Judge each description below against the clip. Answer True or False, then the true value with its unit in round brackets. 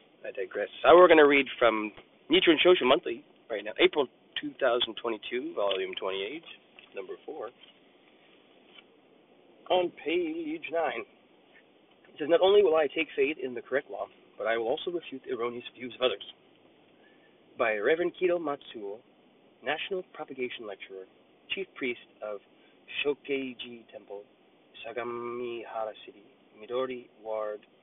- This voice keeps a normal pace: False (130 wpm)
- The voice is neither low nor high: True (165 Hz)